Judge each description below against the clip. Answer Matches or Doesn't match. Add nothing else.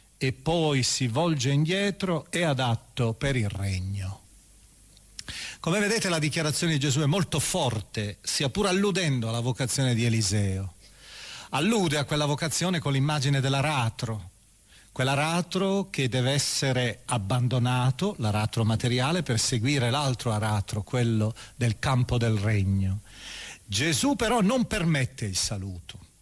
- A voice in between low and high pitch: Doesn't match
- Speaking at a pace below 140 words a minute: Matches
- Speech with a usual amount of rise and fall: Doesn't match